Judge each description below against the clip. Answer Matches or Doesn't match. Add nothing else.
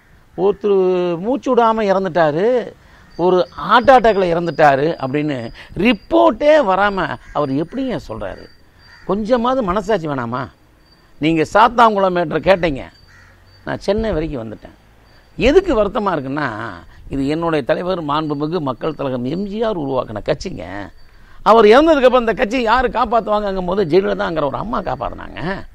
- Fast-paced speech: Doesn't match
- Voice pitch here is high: Doesn't match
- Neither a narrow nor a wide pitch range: Doesn't match